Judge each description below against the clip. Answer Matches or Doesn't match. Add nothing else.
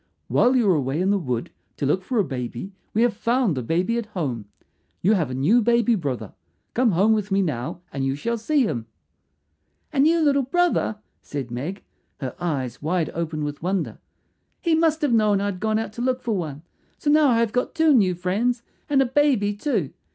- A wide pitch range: Matches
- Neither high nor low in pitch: Doesn't match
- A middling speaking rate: Doesn't match